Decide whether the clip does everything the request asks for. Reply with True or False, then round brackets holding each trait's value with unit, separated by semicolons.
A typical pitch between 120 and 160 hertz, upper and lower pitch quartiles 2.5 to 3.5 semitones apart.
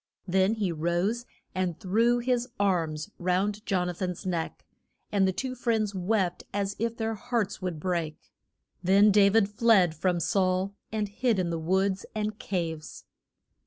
False (195 Hz; 3.2 semitones)